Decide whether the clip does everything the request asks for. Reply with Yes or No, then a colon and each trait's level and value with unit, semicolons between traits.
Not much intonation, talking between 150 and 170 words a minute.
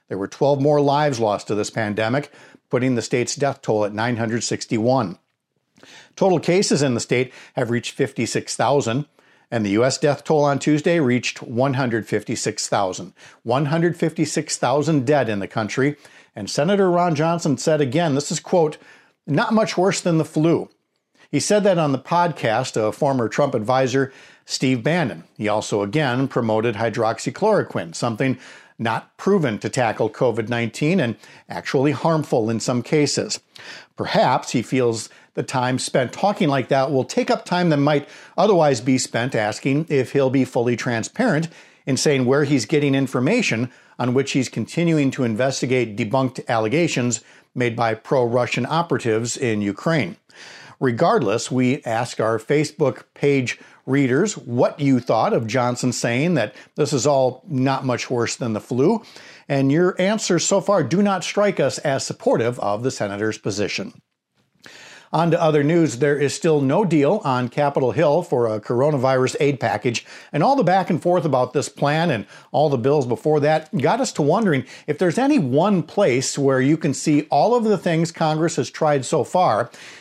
No: average, 4.3 semitones; average, 165 wpm